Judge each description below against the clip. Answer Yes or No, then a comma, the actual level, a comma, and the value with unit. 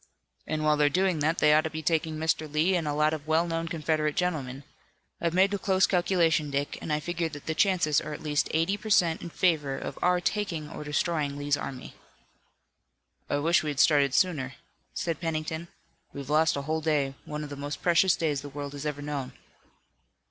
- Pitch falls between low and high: Yes, medium, 155 Hz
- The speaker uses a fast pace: Yes, fast, 210 wpm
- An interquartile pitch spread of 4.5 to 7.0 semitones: No, narrow, 2.5 semitones